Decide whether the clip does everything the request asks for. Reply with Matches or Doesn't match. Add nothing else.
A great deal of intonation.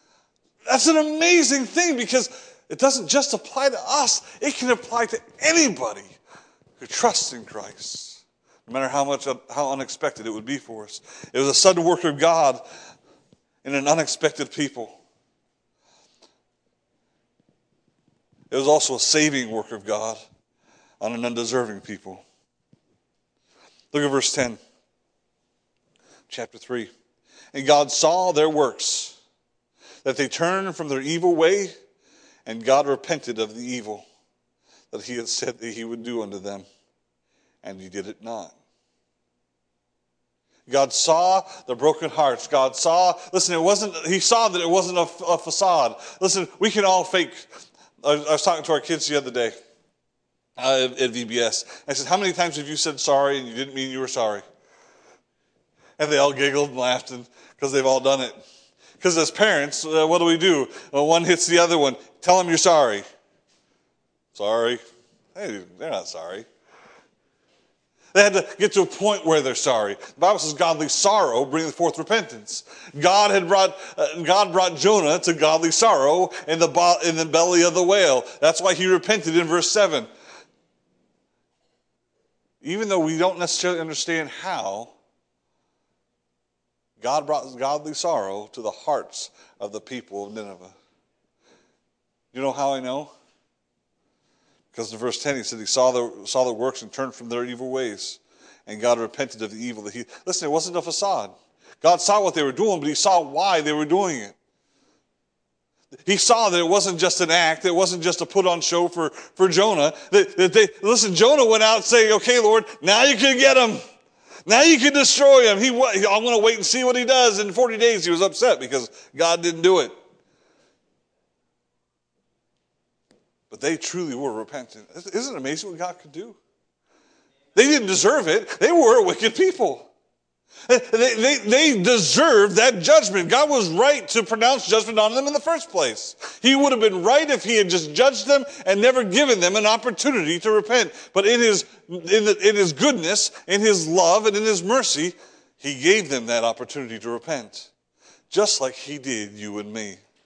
Matches